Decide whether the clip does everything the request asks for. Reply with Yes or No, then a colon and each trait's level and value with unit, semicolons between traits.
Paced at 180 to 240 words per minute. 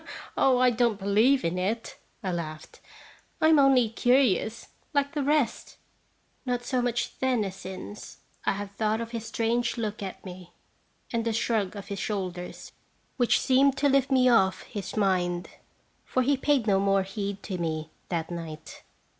No: average, 170 wpm